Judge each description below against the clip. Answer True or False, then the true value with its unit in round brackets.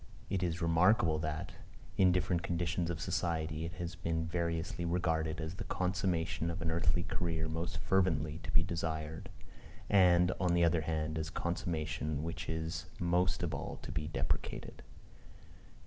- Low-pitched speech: True (85 Hz)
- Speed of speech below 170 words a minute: True (160 wpm)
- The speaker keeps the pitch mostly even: True (1.7 semitones)